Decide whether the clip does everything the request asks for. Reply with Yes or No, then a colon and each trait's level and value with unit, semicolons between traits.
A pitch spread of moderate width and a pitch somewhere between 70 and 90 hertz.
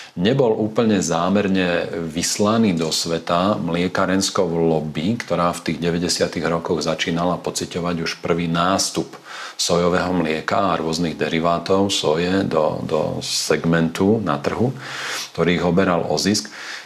No: narrow, 2.2 semitones; very low, 85 Hz